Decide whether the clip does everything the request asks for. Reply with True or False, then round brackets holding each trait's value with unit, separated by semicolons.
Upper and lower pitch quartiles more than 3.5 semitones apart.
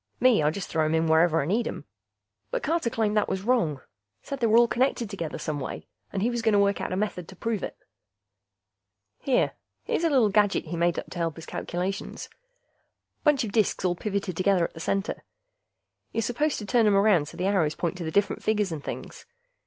True (5.0 semitones)